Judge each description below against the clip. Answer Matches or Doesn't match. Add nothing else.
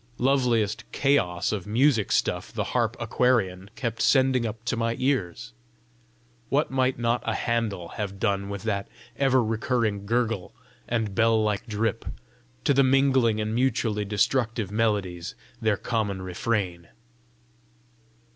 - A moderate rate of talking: Doesn't match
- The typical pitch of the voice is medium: Doesn't match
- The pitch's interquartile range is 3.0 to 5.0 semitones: Matches